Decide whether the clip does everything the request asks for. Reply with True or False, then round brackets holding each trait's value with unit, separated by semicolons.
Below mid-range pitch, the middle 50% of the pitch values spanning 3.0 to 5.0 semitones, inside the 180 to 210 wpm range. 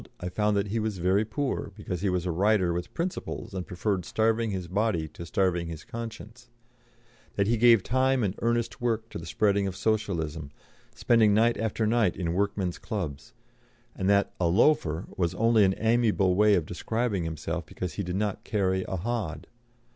True (100 Hz; 3.9 semitones; 185 wpm)